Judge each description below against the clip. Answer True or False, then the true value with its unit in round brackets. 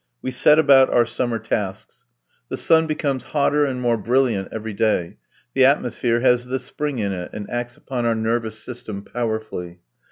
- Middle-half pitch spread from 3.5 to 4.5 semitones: False (3.1 semitones)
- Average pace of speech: True (170 wpm)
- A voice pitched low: True (120 Hz)